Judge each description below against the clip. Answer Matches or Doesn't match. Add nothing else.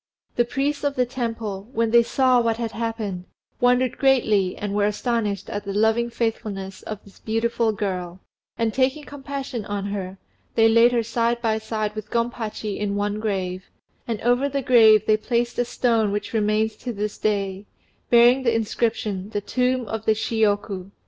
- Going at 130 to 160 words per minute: Doesn't match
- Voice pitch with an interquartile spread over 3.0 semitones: Doesn't match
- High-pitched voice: Matches